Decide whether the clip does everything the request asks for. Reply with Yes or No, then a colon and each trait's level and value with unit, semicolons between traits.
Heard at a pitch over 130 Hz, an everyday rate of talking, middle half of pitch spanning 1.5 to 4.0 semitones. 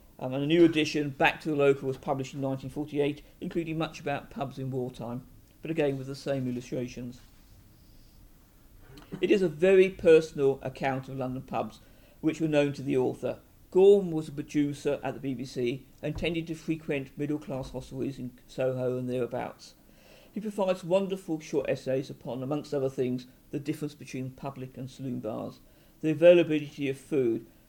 Yes: medium, 140 Hz; average, 170 wpm; average, 3.4 semitones